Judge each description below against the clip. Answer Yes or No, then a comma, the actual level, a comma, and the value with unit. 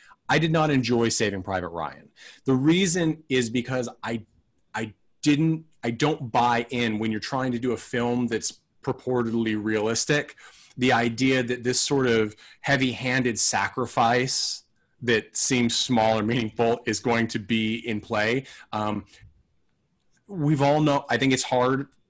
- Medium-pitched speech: No, low, 120 Hz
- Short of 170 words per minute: Yes, average, 150 wpm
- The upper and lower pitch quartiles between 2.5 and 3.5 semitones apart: Yes, average, 2.9 semitones